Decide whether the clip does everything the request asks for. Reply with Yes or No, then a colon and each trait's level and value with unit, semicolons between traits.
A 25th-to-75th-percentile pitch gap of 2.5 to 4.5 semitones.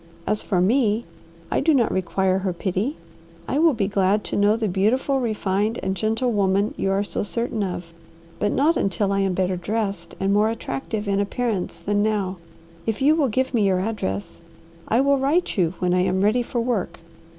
Yes: average, 3.4 semitones